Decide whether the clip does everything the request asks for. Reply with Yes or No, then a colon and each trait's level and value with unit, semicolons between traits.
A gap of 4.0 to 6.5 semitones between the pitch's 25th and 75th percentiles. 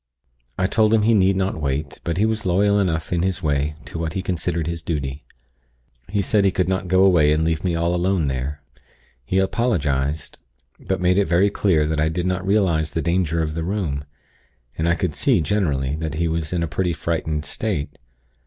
No: average, 3.5 semitones